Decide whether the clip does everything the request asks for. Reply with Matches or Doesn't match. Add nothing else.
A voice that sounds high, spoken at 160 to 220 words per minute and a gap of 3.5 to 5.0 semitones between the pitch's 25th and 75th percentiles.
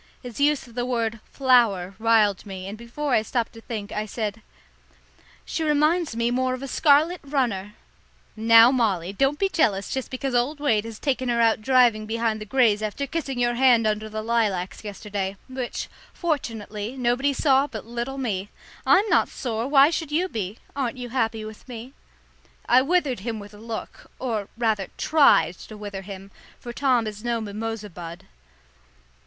Matches